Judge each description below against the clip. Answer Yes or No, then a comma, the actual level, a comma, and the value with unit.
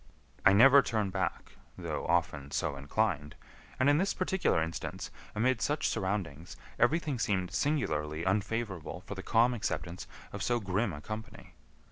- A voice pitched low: Yes, low, 100 Hz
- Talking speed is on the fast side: No, average, 145 wpm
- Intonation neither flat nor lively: No, wide, 5.8 semitones